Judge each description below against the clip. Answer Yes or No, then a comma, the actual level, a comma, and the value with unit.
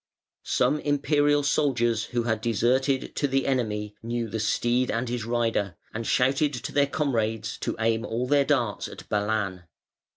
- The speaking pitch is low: Yes, low, 120 Hz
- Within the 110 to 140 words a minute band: No, average, 160 wpm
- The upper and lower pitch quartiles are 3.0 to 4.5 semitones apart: Yes, average, 3.5 semitones